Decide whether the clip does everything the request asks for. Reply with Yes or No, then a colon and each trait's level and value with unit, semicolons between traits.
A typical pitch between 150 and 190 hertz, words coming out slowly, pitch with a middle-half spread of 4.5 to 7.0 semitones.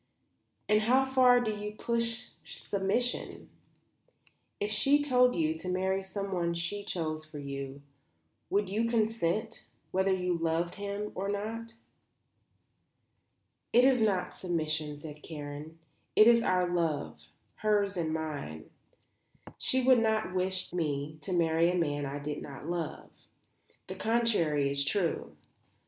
Yes: medium, 185 Hz; slow, 130 wpm; wide, 5.5 semitones